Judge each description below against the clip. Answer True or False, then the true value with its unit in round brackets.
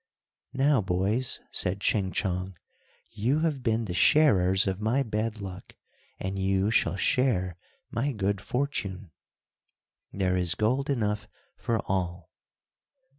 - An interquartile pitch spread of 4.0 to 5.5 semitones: True (4.7 semitones)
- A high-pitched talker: False (100 Hz)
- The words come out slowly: True (125 wpm)